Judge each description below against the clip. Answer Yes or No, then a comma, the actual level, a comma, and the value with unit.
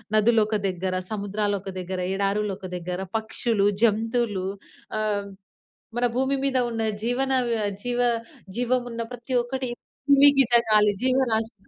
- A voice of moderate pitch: No, high, 225 Hz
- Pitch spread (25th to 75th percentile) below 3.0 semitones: No, average, 3.3 semitones